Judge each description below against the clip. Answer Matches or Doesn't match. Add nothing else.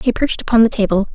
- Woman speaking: Matches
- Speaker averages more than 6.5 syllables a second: Matches